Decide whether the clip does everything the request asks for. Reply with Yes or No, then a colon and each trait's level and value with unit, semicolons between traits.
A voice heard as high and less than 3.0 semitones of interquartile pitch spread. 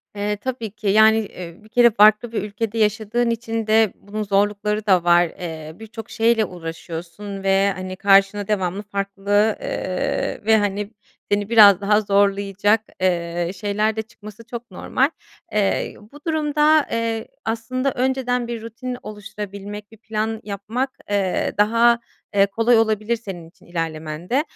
Yes: high, 210 Hz; narrow, 2.4 semitones